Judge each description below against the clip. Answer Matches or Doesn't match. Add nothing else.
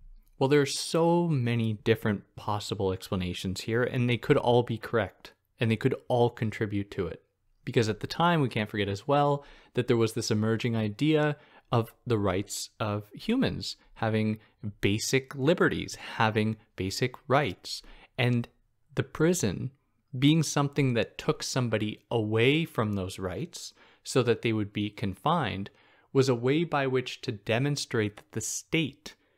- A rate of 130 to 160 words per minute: Matches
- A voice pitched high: Doesn't match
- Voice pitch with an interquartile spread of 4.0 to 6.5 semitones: Matches